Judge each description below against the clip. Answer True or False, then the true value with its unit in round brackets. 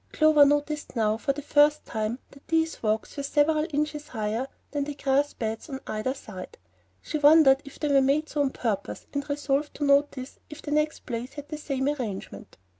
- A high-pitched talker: True (280 Hz)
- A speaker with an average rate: True (195 wpm)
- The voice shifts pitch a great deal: False (2.7 semitones)